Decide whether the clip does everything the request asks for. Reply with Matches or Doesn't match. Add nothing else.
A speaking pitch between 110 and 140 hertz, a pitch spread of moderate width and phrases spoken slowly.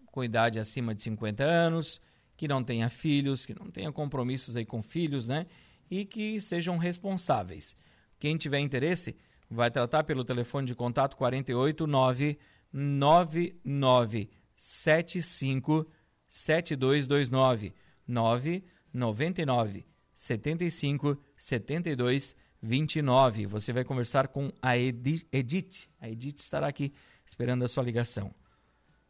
Matches